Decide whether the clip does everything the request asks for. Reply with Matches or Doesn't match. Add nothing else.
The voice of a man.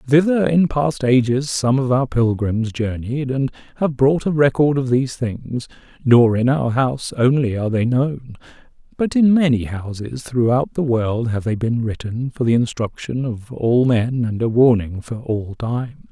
Matches